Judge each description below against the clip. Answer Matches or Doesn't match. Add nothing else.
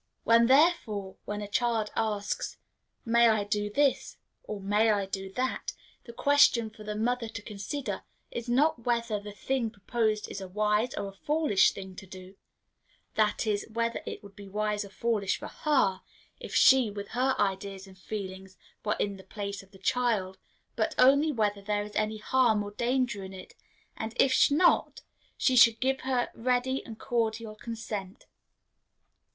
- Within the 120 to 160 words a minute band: Doesn't match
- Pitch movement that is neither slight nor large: Matches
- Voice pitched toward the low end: Doesn't match